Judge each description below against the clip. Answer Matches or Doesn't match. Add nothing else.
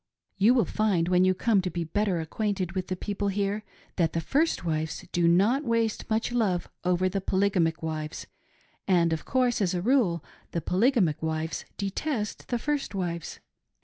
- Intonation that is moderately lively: Matches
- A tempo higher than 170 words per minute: Matches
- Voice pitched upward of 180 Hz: Matches